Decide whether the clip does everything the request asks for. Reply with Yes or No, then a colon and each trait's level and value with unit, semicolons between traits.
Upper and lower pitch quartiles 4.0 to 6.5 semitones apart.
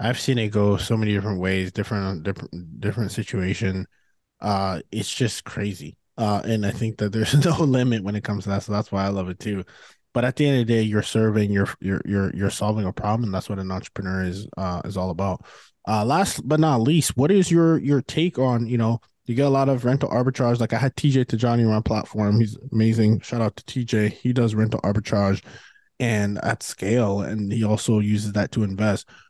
No: average, 3.3 semitones